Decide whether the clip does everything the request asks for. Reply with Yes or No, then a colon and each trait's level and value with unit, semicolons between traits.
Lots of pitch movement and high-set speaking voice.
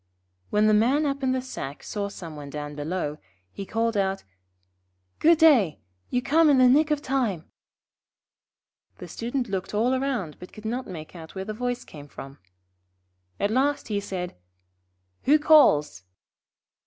Yes: wide, 6.8 semitones; high, 215 Hz